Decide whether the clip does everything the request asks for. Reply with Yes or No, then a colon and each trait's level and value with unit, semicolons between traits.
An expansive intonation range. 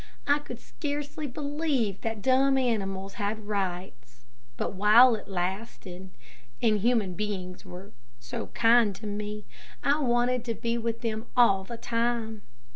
No: average, 3.8 semitones